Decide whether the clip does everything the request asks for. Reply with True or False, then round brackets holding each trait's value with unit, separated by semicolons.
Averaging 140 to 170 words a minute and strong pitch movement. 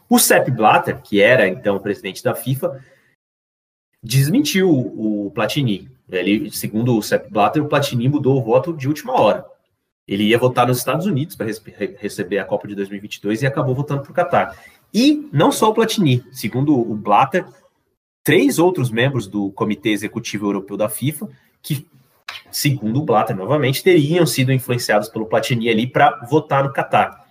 True (165 wpm; 5.8 semitones)